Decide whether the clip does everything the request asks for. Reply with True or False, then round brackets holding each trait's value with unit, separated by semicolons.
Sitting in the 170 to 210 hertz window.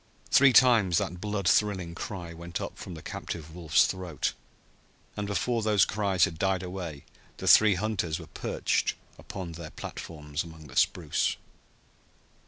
False (90 Hz)